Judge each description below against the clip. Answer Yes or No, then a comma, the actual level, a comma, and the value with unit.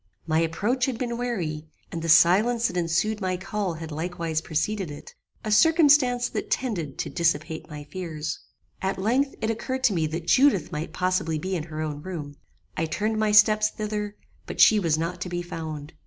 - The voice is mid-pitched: Yes, medium, 180 Hz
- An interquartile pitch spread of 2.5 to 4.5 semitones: No, average, 5.1 semitones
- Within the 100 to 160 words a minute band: No, average, 190 wpm